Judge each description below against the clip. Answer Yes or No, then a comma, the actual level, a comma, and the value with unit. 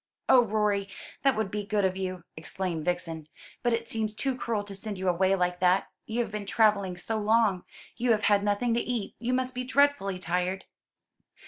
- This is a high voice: Yes, high, 205 Hz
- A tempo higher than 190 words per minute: Yes, average, 200 wpm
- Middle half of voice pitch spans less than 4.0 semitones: Yes, average, 3.5 semitones